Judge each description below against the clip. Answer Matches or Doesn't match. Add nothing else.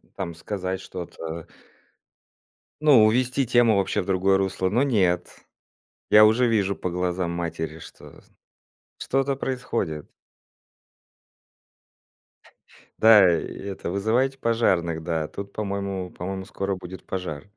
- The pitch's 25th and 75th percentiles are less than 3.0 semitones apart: Doesn't match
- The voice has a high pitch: Doesn't match